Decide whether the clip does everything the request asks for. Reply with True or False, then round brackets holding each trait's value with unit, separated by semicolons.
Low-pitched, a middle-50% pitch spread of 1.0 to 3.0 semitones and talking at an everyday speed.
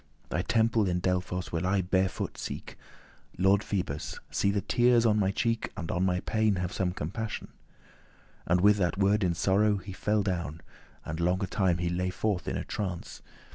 True (95 Hz; 2.6 semitones; 180 wpm)